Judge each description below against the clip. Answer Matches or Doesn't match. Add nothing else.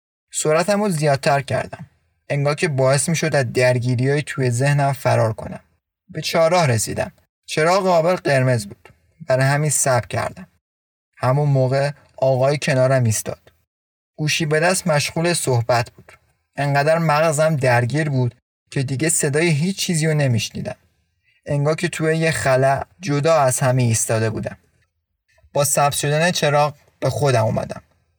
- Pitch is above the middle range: Doesn't match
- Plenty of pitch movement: Doesn't match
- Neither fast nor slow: Matches